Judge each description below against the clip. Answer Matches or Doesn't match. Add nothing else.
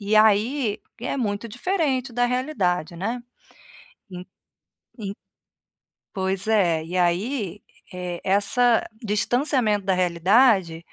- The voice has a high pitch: Matches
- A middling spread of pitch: Matches